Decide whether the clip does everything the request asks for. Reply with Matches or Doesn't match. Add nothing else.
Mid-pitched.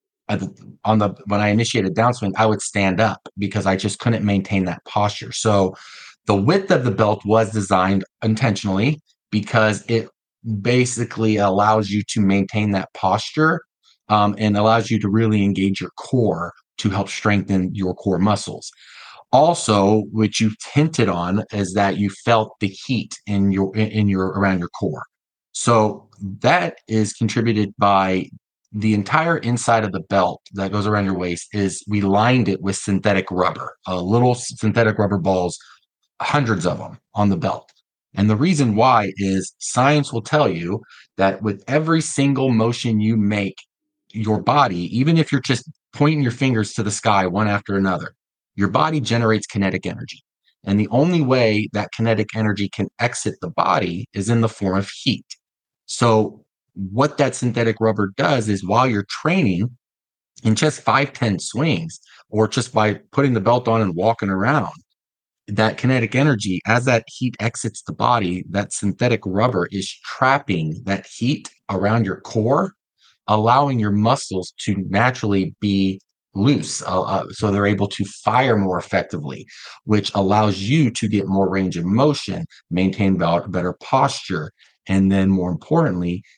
Doesn't match